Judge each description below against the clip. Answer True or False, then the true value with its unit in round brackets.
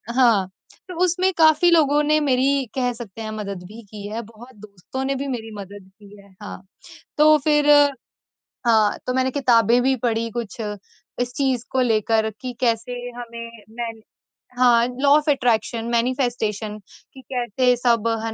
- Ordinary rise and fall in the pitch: True (3.2 semitones)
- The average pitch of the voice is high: True (235 Hz)